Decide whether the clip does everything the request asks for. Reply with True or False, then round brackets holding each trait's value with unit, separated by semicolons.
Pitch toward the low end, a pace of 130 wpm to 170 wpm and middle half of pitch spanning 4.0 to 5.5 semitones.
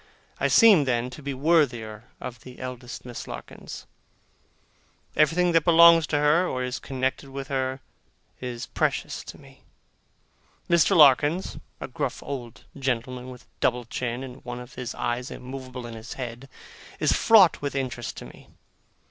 False (130 Hz; 155 wpm; 3.1 semitones)